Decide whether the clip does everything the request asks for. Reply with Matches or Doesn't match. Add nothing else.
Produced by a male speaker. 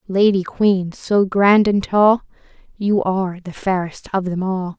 Doesn't match